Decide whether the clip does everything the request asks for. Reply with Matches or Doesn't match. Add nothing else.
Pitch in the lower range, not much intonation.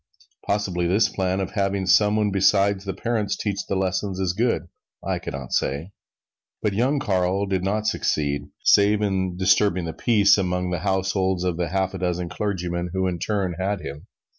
Matches